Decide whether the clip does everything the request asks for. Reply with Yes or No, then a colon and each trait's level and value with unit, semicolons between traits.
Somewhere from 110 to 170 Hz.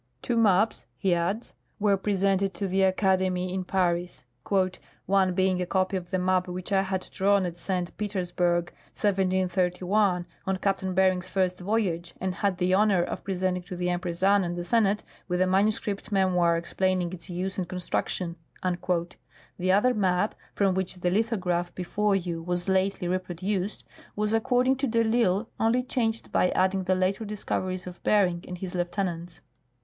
No: medium, 185 Hz